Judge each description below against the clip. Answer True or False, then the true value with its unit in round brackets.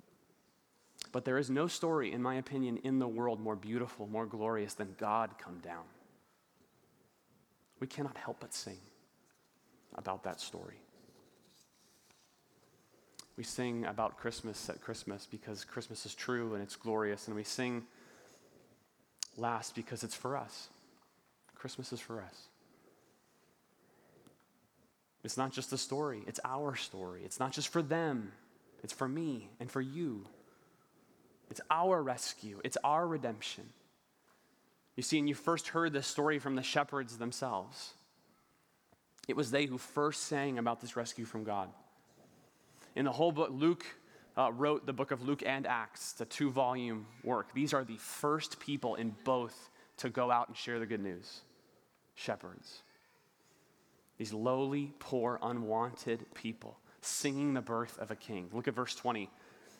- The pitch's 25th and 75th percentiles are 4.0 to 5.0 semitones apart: False (3.6 semitones)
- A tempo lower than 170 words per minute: True (150 wpm)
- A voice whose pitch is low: True (120 Hz)